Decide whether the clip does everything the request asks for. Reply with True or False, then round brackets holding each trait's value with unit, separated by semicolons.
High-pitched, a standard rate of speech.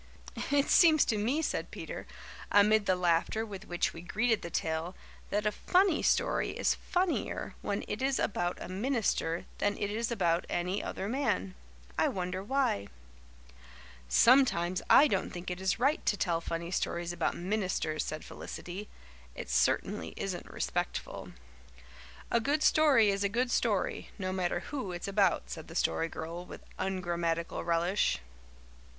True (195 Hz; 155 wpm)